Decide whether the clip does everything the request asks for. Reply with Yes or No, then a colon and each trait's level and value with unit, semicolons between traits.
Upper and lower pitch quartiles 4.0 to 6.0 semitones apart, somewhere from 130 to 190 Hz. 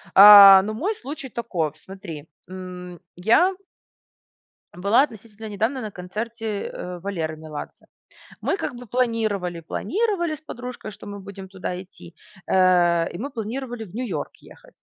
No: average, 5.0 semitones; high, 205 Hz